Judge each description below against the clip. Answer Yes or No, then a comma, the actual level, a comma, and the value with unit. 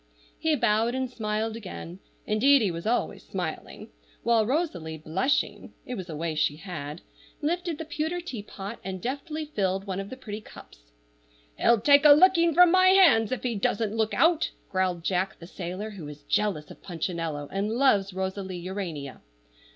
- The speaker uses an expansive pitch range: Yes, wide, 6.7 semitones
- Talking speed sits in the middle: Yes, average, 170 wpm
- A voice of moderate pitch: No, high, 210 Hz